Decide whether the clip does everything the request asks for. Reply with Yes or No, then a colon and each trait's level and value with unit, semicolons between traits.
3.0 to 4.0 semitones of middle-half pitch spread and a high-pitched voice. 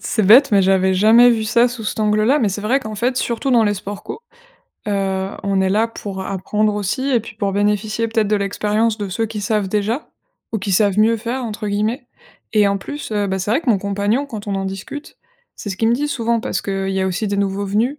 No: narrow, 2.6 semitones; high, 210 Hz